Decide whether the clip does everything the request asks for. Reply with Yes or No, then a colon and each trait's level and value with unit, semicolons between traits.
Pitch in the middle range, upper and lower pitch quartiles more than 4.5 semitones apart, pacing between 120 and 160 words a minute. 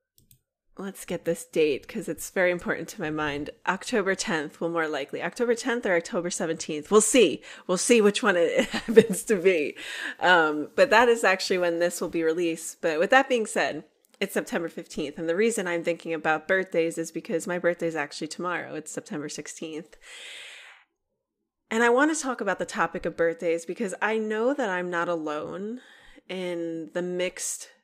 No: medium, 180 Hz; average, 5.1 semitones; average, 185 wpm